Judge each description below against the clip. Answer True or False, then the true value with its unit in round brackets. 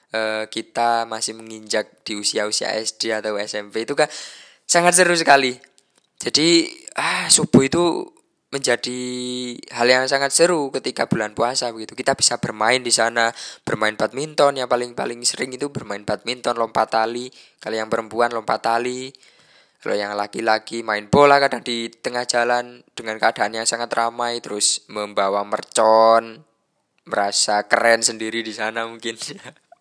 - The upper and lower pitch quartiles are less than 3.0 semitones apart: True (2.4 semitones)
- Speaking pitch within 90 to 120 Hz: True (115 Hz)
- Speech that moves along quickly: False (135 wpm)